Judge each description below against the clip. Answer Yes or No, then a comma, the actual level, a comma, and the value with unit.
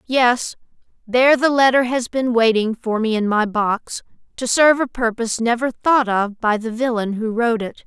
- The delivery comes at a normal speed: Yes, average, 190 wpm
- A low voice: No, high, 235 Hz